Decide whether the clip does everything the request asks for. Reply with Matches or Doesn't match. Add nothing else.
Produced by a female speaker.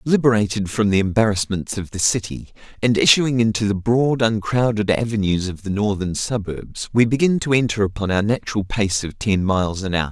Doesn't match